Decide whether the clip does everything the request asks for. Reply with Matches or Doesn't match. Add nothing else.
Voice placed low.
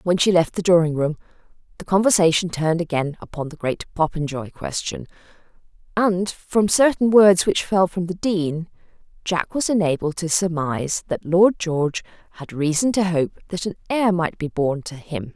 Doesn't match